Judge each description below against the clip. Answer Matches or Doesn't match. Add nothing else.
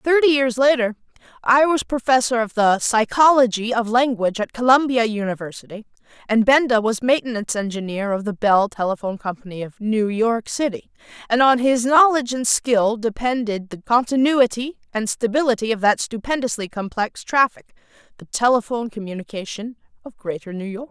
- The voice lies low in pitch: Doesn't match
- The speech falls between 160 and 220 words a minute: Doesn't match